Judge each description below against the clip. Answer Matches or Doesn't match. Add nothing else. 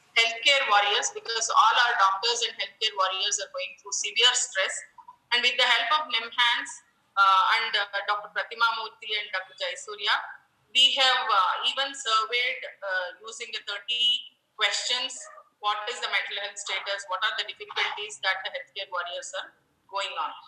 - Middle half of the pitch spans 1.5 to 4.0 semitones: Doesn't match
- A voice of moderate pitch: Doesn't match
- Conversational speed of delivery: Matches